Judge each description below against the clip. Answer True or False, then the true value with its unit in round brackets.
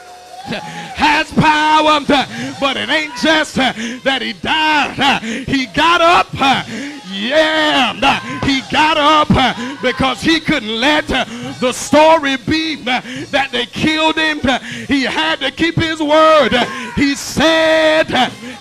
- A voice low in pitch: False (285 Hz)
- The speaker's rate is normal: False (115 wpm)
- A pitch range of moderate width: True (3.6 semitones)